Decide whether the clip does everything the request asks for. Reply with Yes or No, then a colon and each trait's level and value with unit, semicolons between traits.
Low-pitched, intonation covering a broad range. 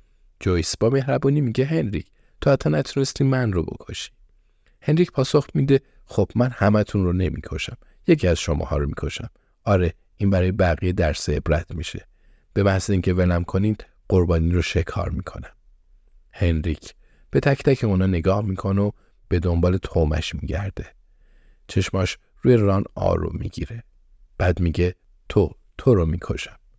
No: very low, 95 Hz; average, 4.0 semitones